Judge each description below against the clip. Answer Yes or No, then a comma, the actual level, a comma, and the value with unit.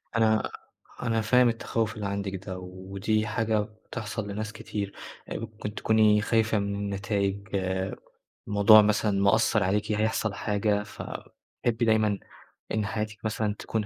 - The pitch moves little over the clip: Yes, narrow, 1.4 semitones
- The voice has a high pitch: No, low, 105 Hz